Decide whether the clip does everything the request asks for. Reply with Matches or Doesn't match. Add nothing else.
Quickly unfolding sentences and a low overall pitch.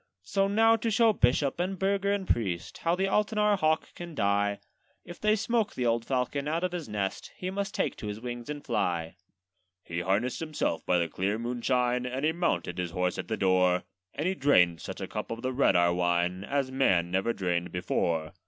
Matches